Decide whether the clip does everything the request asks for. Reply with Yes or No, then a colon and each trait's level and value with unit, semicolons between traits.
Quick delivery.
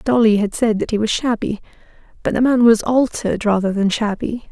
No: average, 185 wpm